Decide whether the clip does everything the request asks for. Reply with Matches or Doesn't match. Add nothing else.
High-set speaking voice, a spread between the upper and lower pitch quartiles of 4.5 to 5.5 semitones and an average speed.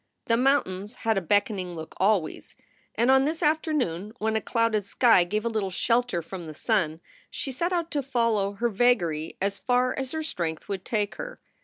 Matches